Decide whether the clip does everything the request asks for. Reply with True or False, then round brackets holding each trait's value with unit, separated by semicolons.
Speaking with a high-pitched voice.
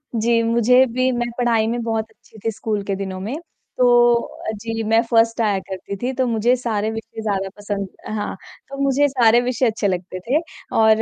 True (225 Hz)